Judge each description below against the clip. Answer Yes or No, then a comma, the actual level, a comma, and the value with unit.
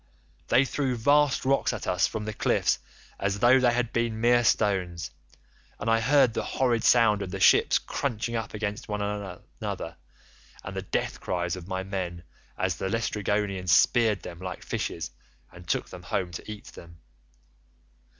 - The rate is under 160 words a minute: No, average, 170 wpm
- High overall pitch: No, low, 105 Hz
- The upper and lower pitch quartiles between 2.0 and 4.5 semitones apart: Yes, average, 4.1 semitones